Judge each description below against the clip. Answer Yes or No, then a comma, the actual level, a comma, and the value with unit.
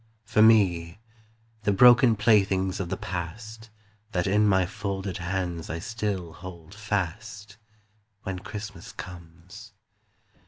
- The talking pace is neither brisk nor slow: No, slow, 115 wpm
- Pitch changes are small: No, average, 3.1 semitones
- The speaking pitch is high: No, very low, 95 Hz